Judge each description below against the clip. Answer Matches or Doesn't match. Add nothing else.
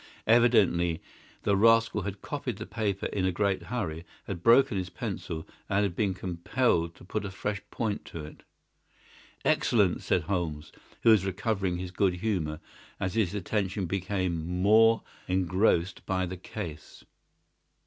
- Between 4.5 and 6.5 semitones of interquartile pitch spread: Doesn't match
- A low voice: Matches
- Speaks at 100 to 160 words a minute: Matches